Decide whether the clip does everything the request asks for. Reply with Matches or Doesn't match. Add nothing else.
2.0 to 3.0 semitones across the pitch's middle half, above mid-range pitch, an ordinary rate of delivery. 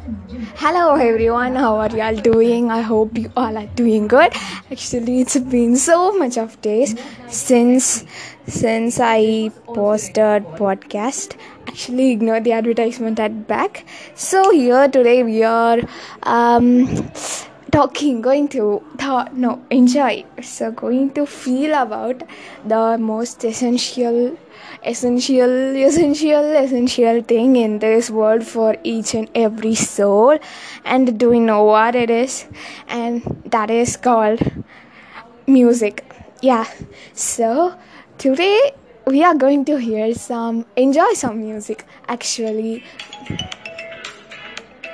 Matches